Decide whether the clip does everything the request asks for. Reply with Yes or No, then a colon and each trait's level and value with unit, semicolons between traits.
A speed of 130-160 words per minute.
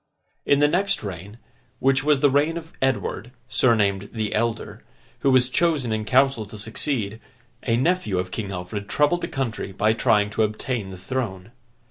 No: average, 170 wpm